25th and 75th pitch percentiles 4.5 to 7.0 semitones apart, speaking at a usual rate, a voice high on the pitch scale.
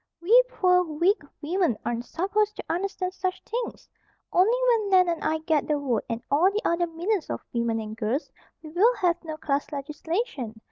Yes: average, 5.3 semitones; average, 185 wpm; very high, 340 Hz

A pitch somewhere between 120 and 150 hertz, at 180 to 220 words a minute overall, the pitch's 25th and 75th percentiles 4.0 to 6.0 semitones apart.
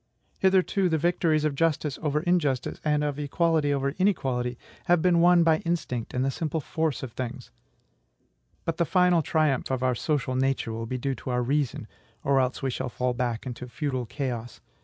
Yes: medium, 140 Hz; average, 185 wpm; average, 4.3 semitones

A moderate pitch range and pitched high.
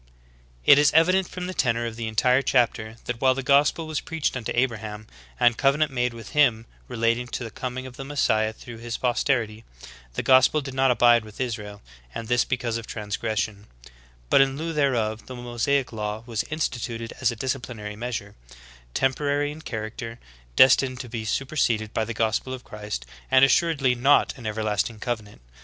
No: average, 3.3 semitones; low, 120 Hz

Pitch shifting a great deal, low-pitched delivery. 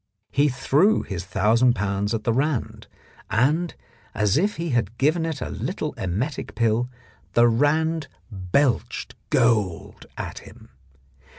Yes: wide, 5.9 semitones; low, 120 Hz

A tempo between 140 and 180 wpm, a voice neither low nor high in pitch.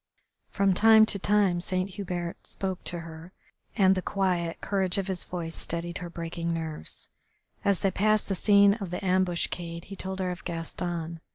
Yes: average, 175 wpm; medium, 180 Hz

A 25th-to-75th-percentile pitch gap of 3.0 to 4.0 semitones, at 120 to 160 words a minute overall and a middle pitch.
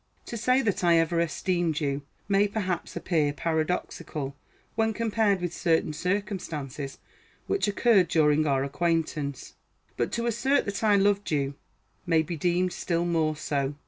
No: average, 4.8 semitones; average, 145 wpm; medium, 170 Hz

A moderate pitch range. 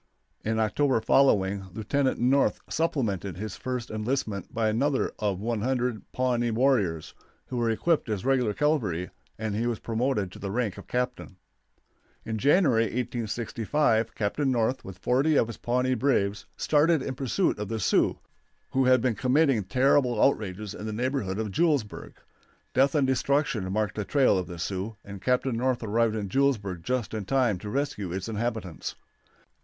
Yes: average, 4.1 semitones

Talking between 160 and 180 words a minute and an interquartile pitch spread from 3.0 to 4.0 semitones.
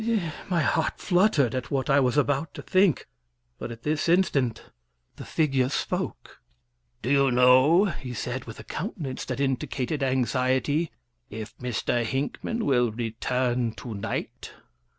No: average, 140 wpm; average, 3.6 semitones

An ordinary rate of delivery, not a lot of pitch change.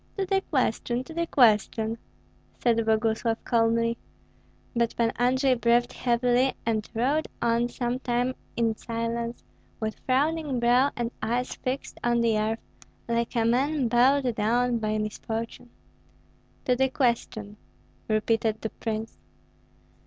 No: slow, 130 wpm; narrow, 1.9 semitones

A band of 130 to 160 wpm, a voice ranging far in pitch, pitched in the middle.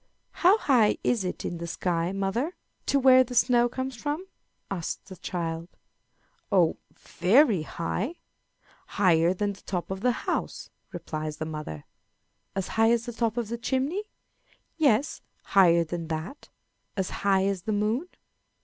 No: average, 150 wpm; wide, 6.2 semitones; high, 205 Hz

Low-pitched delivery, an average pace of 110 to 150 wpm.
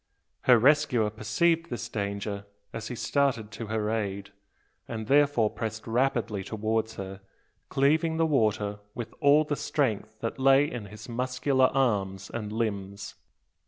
Yes: low, 115 Hz; average, 140 wpm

